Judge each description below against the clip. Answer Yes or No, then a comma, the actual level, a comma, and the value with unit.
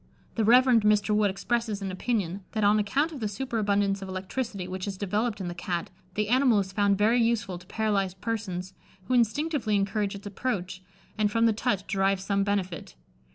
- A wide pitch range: No, average, 2.8 semitones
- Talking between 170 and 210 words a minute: Yes, average, 190 wpm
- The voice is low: No, high, 205 Hz